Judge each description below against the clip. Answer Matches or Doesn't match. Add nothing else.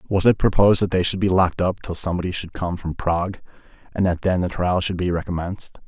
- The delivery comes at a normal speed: Doesn't match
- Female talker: Doesn't match